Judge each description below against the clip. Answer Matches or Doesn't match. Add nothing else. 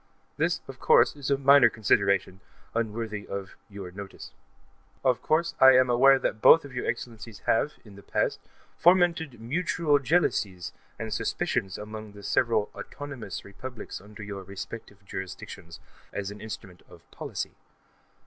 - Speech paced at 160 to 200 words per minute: Doesn't match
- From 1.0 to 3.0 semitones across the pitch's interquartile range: Doesn't match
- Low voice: Matches